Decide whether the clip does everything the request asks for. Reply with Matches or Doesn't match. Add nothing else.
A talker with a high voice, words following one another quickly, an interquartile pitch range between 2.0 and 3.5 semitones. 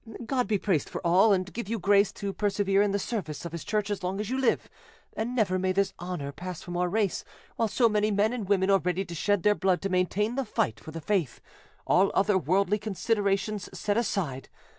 Matches